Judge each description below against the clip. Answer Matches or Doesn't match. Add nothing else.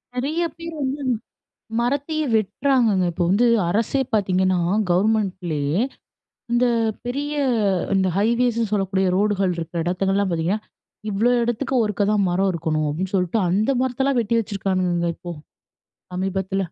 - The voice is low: Doesn't match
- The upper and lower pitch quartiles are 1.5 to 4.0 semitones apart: Doesn't match